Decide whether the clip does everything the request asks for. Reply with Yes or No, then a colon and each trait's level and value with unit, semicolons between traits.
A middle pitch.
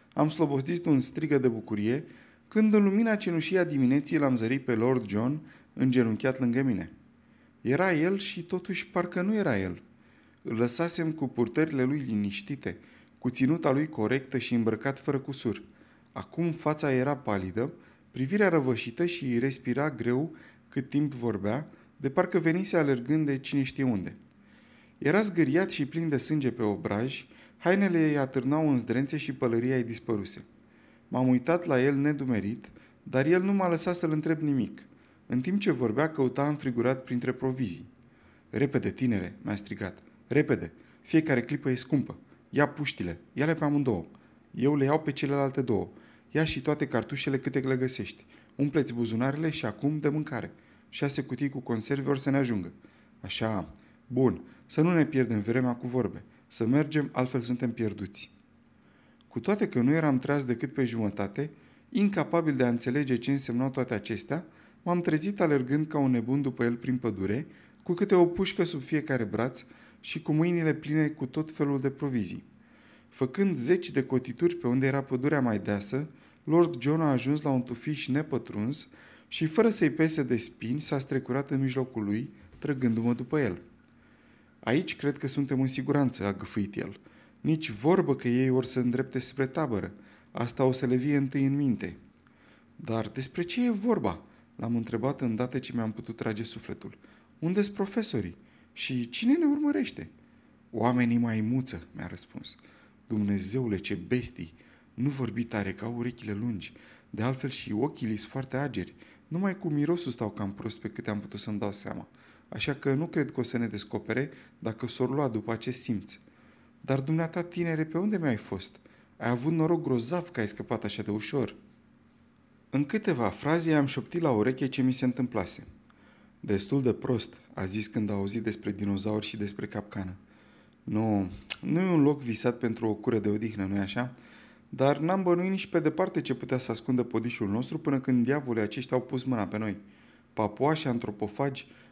No: low, 130 Hz